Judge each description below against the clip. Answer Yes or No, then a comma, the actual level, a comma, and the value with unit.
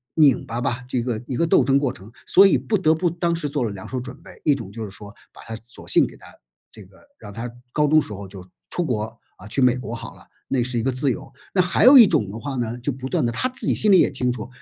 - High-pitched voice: No, low, 125 Hz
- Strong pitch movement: No, average, 4.8 semitones